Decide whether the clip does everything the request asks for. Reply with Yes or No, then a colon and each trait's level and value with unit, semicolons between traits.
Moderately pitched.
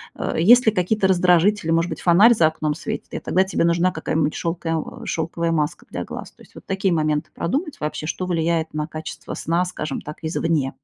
Yes: medium, 170 Hz